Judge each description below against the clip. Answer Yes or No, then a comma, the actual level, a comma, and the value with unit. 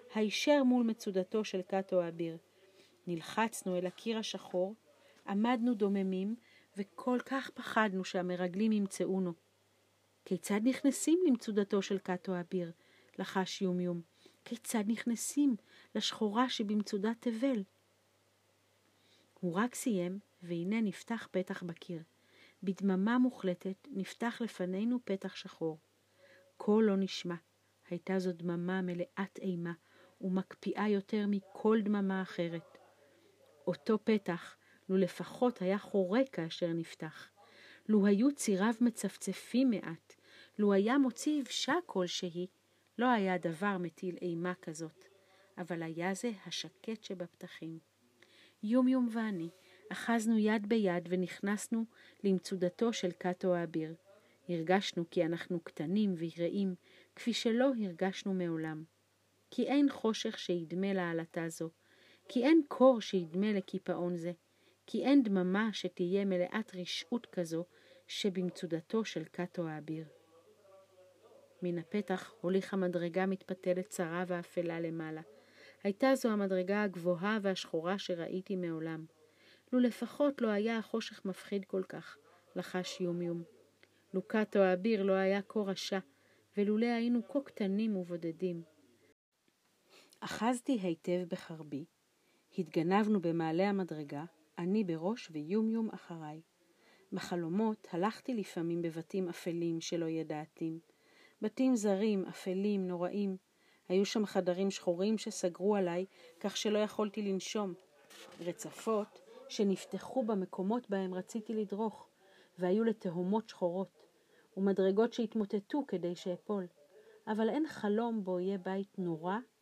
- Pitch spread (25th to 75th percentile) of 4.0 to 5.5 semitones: No, average, 3.6 semitones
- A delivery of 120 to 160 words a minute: No, average, 110 wpm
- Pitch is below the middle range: No, high, 190 Hz